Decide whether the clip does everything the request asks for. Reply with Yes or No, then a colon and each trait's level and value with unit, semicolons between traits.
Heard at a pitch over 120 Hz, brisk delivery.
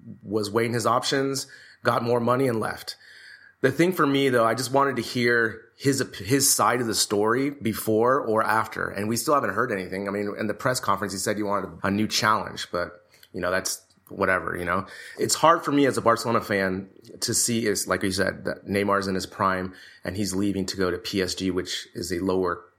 No: low, 105 Hz; fast, 220 wpm